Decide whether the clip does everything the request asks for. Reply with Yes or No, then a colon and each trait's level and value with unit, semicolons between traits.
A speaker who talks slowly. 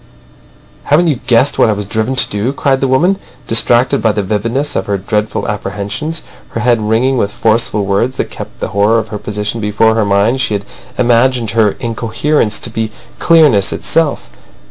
No: average, 185 wpm